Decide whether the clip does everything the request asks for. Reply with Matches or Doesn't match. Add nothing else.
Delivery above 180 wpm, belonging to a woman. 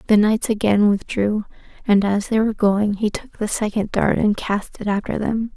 Matches